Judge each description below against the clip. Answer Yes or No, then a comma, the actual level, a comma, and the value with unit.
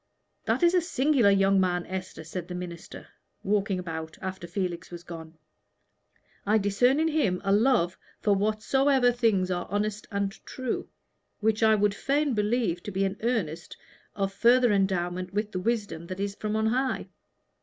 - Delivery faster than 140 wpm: Yes, average, 165 wpm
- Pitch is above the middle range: Yes, high, 200 Hz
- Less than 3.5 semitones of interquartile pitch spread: No, average, 3.9 semitones